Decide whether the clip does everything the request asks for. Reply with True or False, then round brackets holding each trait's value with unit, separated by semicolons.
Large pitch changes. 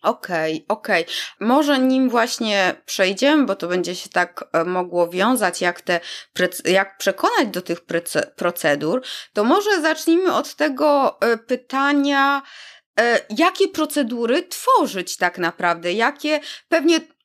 True (8.6 semitones)